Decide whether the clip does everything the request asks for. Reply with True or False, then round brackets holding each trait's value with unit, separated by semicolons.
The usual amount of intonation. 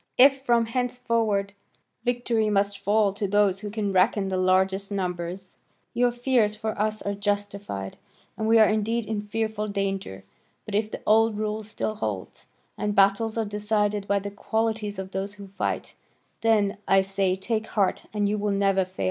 False (1.9 semitones)